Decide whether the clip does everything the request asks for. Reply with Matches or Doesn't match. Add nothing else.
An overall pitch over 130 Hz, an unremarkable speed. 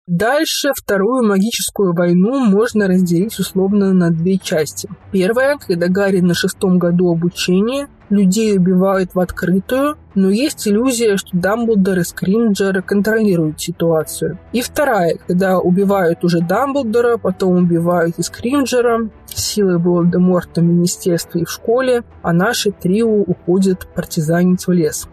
Matches